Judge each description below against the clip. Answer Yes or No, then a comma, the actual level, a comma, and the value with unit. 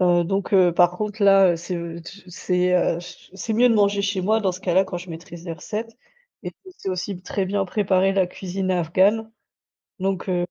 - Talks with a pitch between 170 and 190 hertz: Yes, medium, 185 Hz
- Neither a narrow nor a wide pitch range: No, narrow, 2.2 semitones